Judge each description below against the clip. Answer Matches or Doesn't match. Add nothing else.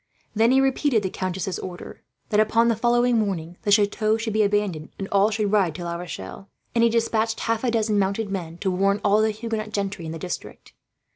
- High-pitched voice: Matches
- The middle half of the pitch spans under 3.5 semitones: Matches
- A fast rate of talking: Matches